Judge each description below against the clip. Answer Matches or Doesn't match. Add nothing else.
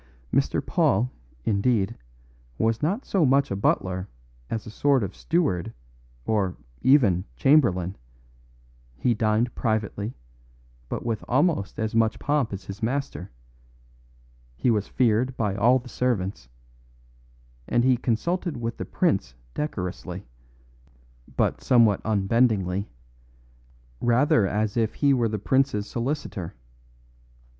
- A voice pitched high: Doesn't match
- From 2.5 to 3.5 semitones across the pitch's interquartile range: Doesn't match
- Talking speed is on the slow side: Matches